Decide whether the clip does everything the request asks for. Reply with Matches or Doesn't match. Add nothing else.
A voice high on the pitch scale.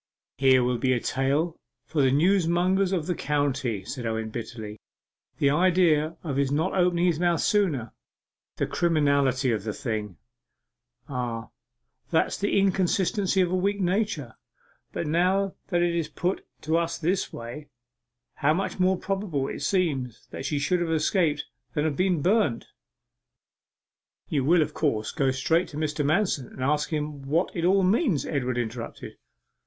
Doesn't match